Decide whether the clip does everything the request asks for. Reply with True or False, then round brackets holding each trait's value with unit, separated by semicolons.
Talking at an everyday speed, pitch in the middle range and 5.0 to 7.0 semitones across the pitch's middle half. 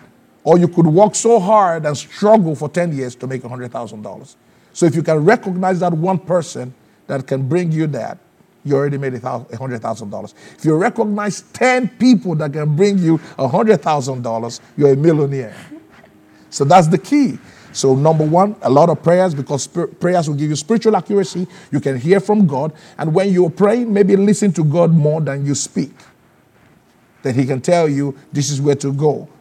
True (180 wpm; 165 Hz; 5.3 semitones)